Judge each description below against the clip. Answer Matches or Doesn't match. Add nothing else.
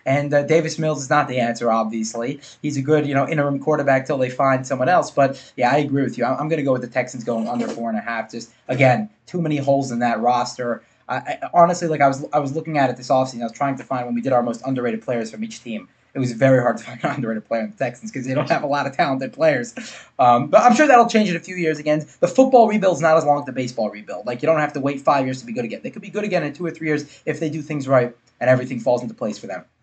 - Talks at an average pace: Doesn't match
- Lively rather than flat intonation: Doesn't match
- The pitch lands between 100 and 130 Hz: Doesn't match